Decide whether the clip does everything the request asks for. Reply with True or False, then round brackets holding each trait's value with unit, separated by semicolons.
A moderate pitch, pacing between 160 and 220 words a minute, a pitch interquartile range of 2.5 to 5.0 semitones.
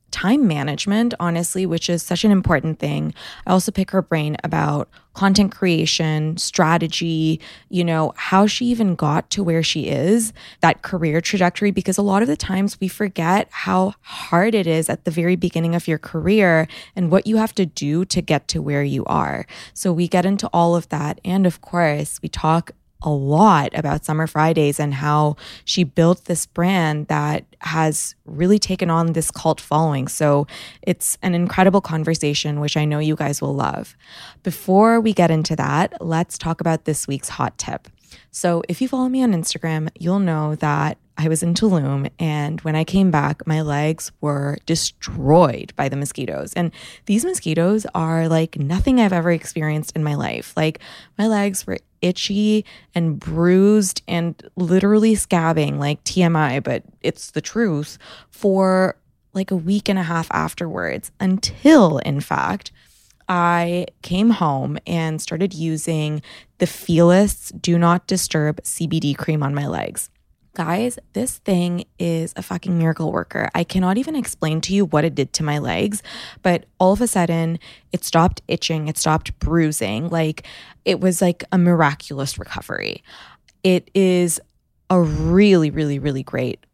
True (170 Hz; 170 wpm; 3.3 semitones)